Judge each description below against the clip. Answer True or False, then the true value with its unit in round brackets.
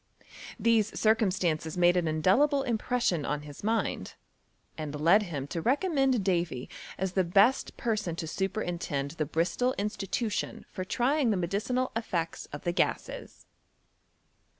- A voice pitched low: False (190 Hz)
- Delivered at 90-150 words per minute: True (135 wpm)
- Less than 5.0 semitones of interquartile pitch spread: False (5.5 semitones)